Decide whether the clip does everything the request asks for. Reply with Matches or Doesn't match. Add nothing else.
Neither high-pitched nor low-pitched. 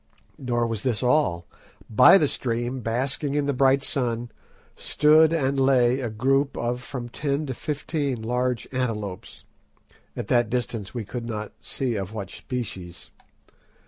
Doesn't match